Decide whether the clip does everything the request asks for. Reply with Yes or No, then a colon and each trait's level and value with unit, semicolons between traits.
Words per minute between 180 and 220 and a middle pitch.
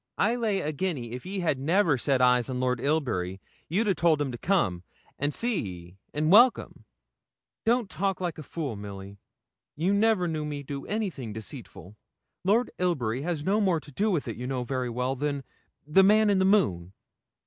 Yes: average, 190 wpm; medium, 150 Hz